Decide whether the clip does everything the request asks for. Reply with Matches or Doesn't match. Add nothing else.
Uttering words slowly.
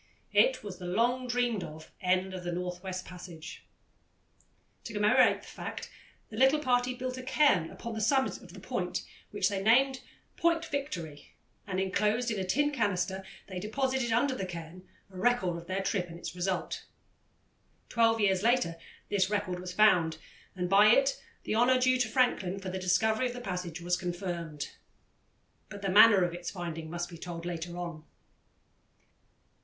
Doesn't match